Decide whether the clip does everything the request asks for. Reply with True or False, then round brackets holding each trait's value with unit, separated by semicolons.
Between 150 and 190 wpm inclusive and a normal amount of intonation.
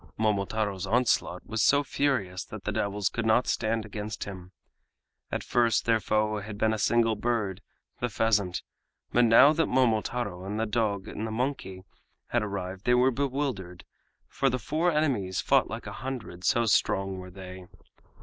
True (170 wpm; 3.9 semitones)